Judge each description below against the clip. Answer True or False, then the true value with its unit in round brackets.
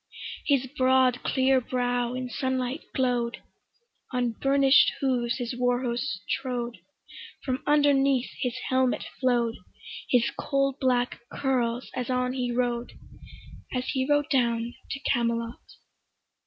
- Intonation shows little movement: True (1.6 semitones)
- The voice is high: True (250 Hz)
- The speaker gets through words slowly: True (120 wpm)